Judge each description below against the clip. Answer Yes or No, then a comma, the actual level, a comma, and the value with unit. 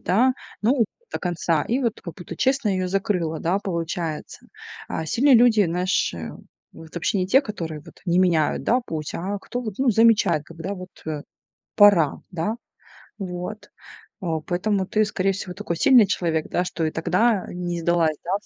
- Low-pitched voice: No, medium, 185 Hz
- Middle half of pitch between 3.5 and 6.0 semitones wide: Yes, average, 4.1 semitones